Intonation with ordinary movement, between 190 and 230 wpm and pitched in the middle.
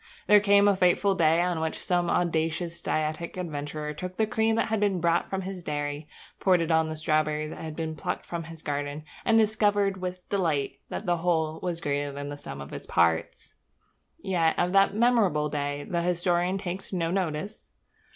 Yes: average, 3.7 semitones; average, 195 wpm; medium, 170 Hz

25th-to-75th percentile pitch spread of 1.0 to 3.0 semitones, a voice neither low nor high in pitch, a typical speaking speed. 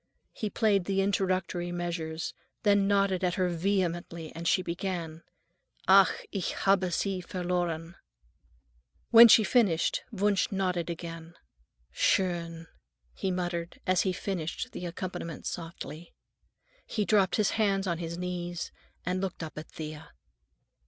No: narrow, 2.4 semitones; medium, 180 Hz; slow, 130 wpm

